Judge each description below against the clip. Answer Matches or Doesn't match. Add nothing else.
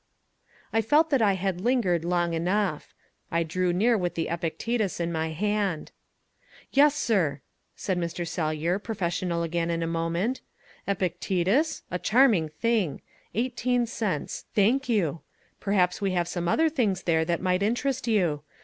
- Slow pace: Doesn't match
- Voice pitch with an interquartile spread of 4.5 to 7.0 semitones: Matches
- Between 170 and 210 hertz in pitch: Matches